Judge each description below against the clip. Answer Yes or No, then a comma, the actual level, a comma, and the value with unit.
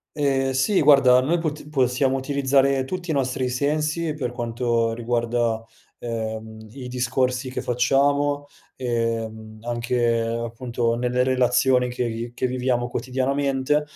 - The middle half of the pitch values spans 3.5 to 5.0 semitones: No, narrow, 2.6 semitones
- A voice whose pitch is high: No, low, 125 Hz